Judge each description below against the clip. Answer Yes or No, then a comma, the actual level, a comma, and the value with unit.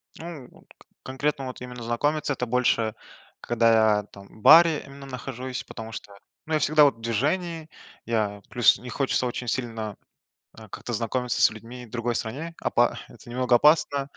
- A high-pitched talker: No, low, 125 Hz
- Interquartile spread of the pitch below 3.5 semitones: No, average, 3.8 semitones